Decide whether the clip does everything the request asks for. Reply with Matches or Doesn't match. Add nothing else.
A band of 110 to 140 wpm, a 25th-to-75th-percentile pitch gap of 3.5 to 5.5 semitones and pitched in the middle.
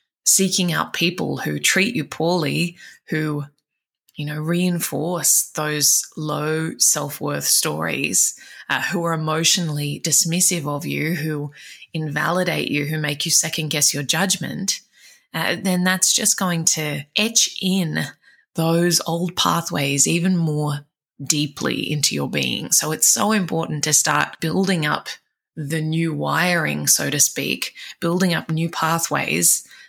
Doesn't match